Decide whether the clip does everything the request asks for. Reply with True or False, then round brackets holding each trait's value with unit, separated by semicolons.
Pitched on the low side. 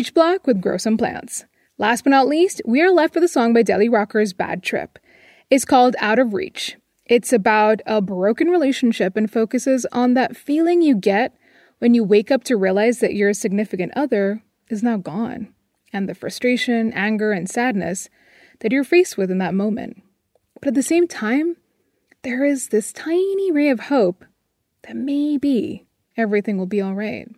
False (235 Hz)